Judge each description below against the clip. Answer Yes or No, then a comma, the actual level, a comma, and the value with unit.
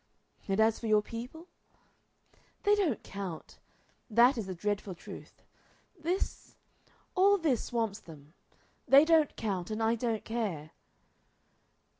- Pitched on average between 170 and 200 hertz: No, high, 225 Hz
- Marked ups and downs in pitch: Yes, wide, 6.0 semitones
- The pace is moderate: No, slow, 125 wpm